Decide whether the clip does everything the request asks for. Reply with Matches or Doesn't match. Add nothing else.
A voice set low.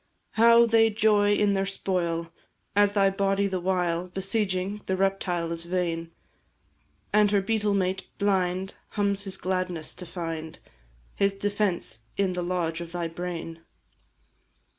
Doesn't match